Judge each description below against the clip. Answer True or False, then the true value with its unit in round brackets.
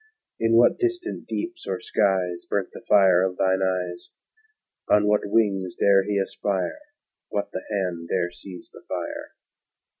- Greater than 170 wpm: False (150 wpm)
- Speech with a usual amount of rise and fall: False (2.3 semitones)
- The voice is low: True (95 Hz)